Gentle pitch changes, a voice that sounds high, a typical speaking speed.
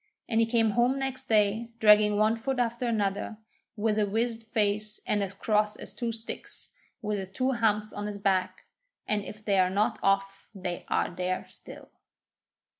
Yes: narrow, 2.2 semitones; high, 210 Hz; average, 180 wpm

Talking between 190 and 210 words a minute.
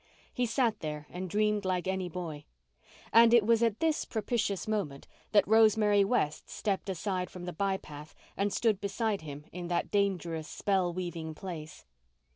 No: average, 165 wpm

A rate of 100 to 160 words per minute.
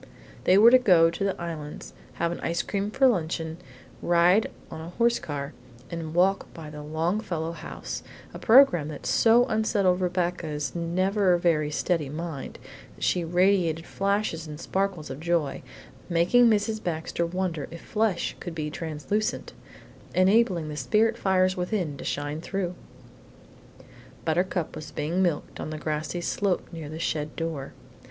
Yes: average, 150 wpm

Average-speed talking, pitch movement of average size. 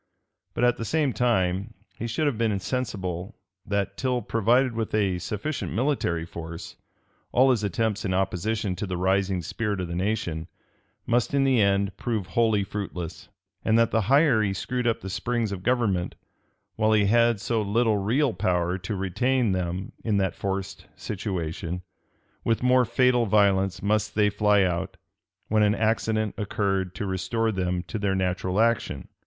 Yes: average, 165 wpm; average, 3.6 semitones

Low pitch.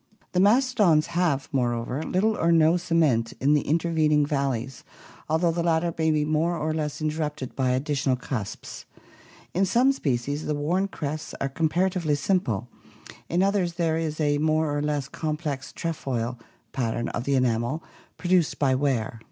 No: medium, 155 Hz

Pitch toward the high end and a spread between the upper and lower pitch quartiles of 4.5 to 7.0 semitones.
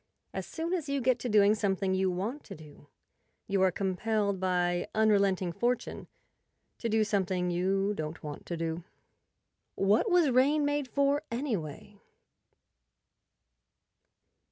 Yes: high, 200 Hz; wide, 5.4 semitones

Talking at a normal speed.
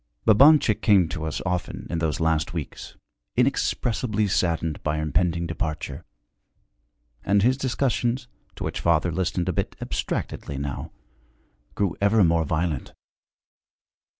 No: slow, 125 wpm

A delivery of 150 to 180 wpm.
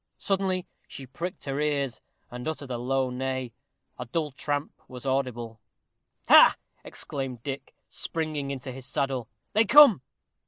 No: slow, 135 wpm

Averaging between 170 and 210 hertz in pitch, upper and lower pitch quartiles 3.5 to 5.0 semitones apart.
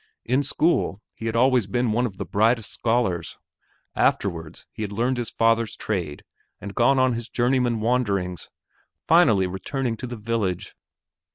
No: low, 115 Hz; average, 3.8 semitones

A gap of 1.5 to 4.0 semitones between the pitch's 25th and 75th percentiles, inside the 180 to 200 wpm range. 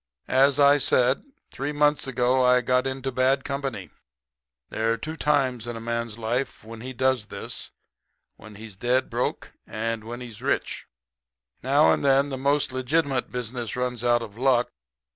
No: narrow, 2.4 semitones; average, 165 wpm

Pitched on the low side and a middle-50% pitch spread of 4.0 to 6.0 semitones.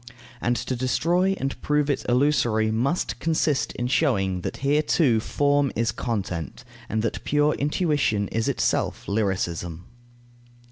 Yes: low, 125 Hz; average, 5.1 semitones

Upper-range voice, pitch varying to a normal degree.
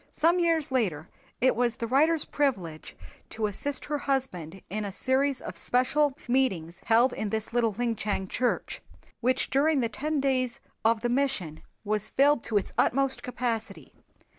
Yes: high, 245 Hz; average, 4.3 semitones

